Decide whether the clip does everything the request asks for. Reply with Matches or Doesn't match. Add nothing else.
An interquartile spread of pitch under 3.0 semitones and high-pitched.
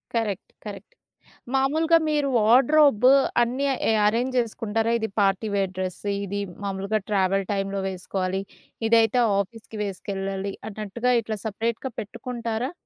Doesn't match